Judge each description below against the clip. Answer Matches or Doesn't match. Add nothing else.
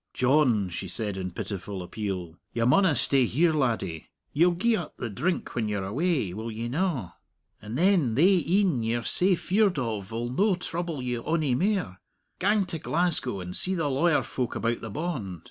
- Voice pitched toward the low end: Matches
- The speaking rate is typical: Matches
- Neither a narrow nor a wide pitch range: Doesn't match